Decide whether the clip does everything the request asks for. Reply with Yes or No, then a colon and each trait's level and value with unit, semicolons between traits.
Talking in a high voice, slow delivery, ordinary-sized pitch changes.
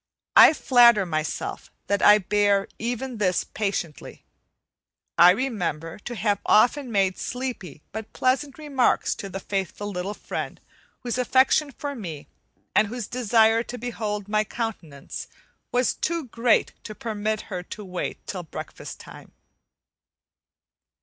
Yes: high, 215 Hz; slow, 130 wpm; average, 4.1 semitones